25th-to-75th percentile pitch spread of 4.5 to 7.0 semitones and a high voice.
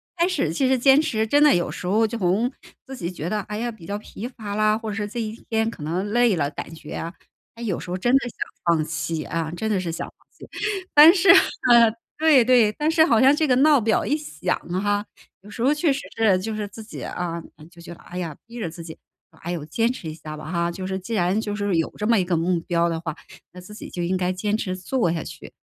Yes: wide, 5.4 semitones; high, 205 Hz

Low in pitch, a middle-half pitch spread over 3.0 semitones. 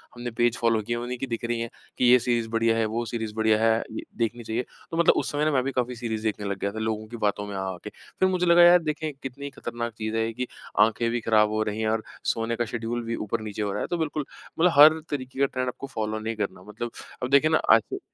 No: low, 115 Hz; average, 2.7 semitones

